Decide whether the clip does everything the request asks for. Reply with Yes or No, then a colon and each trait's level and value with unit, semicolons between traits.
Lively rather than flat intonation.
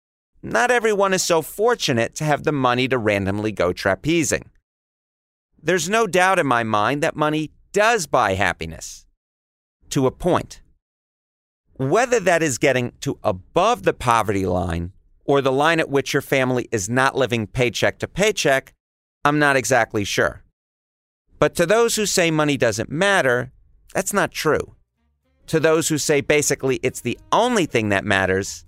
Yes: wide, 8.4 semitones